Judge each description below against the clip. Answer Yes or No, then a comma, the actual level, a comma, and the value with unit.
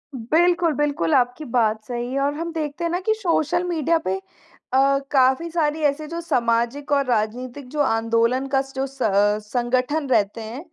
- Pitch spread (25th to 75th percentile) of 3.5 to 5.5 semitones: Yes, average, 4.4 semitones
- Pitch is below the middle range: No, very high, 275 Hz